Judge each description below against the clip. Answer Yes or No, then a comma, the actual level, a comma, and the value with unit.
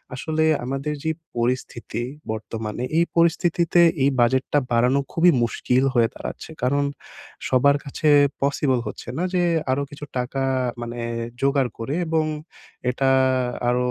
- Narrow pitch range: No, average, 3.7 semitones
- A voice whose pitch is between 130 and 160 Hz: Yes, low, 135 Hz